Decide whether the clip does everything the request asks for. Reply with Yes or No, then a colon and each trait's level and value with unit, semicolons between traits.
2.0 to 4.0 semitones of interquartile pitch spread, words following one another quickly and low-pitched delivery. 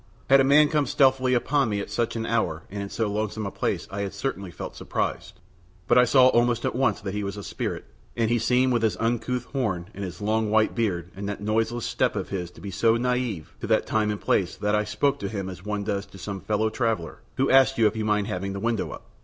Yes: average, 3.3 semitones; fast, 255 wpm; low, 110 Hz